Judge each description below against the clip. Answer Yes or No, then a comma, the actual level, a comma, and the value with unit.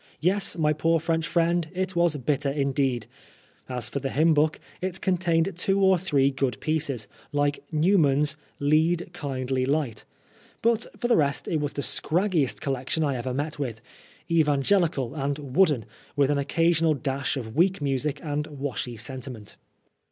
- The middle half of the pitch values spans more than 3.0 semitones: Yes, average, 3.5 semitones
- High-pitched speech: No, medium, 150 Hz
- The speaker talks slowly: No, average, 165 wpm